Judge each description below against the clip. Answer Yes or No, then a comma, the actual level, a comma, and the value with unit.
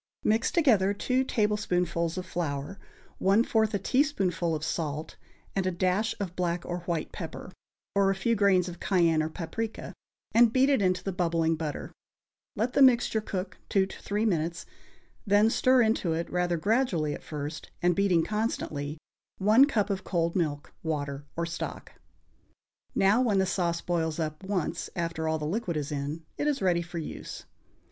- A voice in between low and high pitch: Yes, medium, 180 Hz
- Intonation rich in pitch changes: No, average, 4.3 semitones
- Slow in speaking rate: No, average, 170 wpm